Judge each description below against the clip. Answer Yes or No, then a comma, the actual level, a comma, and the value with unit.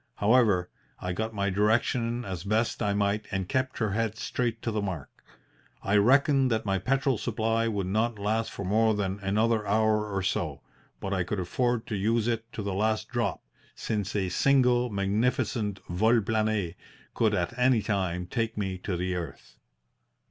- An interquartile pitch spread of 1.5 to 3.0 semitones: Yes, average, 2.7 semitones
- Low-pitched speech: Yes, low, 105 Hz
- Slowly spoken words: No, average, 175 wpm